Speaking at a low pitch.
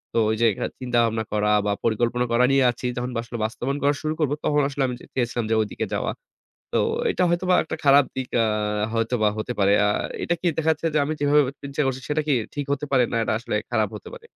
Yes: low, 125 Hz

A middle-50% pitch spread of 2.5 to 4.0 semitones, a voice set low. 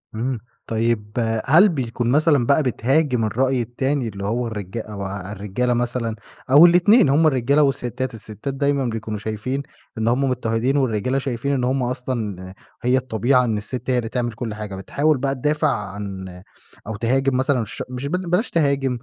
Yes: average, 3.7 semitones; low, 125 Hz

